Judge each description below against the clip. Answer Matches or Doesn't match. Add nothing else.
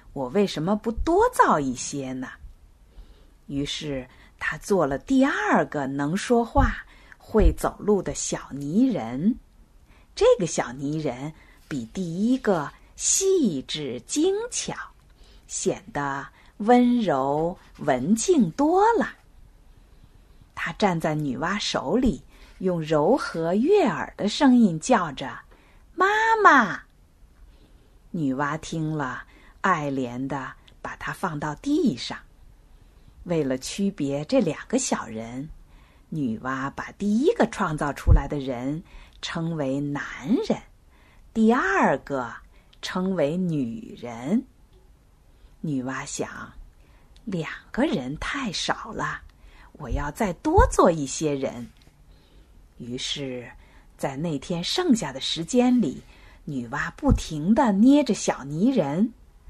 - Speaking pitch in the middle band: Matches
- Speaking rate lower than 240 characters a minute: Matches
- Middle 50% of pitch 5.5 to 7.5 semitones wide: Doesn't match